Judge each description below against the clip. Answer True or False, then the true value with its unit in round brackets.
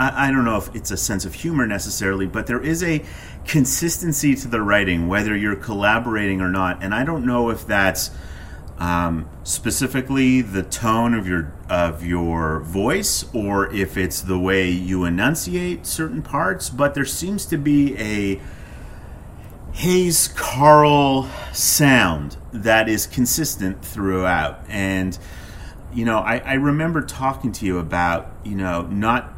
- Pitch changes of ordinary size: False (6.7 semitones)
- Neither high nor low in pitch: False (100 Hz)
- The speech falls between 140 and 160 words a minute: True (150 wpm)